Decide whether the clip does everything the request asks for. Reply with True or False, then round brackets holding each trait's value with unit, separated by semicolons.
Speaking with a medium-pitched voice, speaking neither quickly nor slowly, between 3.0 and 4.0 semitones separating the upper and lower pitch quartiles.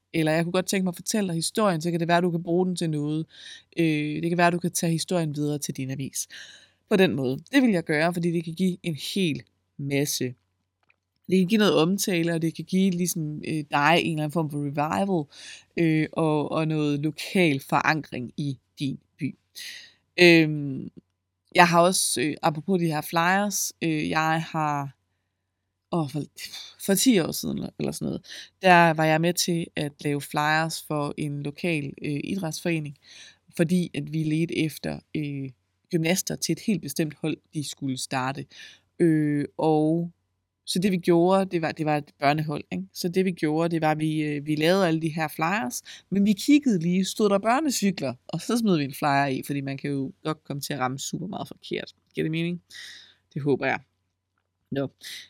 True (160 Hz; 195 wpm; 3.5 semitones)